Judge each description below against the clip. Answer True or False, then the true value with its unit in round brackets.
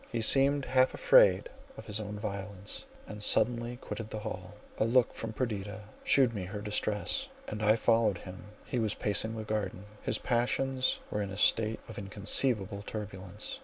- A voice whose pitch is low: True (110 Hz)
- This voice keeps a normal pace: True (170 wpm)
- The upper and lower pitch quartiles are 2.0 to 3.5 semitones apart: True (2.5 semitones)